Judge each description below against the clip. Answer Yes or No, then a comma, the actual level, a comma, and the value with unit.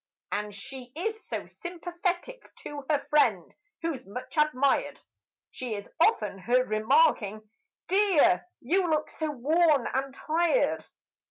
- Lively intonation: Yes, wide, 6.3 semitones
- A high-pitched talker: Yes, very high, 295 Hz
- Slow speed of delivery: Yes, slow, 120 wpm